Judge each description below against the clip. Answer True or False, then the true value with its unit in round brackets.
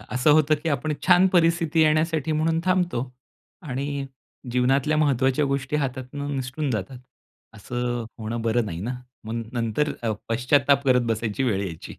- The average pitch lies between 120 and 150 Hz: True (135 Hz)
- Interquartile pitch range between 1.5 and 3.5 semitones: False (4.1 semitones)